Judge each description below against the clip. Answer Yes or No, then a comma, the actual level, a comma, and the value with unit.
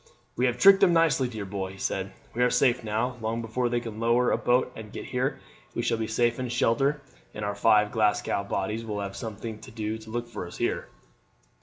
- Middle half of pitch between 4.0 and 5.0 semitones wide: No, narrow, 2.5 semitones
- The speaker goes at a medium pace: No, fast, 225 wpm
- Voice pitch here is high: No, low, 115 Hz